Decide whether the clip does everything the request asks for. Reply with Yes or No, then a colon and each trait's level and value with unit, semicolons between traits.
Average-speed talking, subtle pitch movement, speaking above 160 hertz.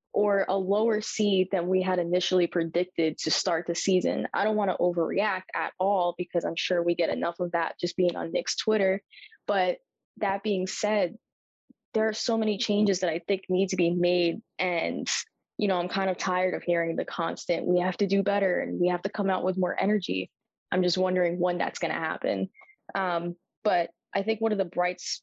No: fast, 215 wpm; narrow, 2.2 semitones; medium, 185 Hz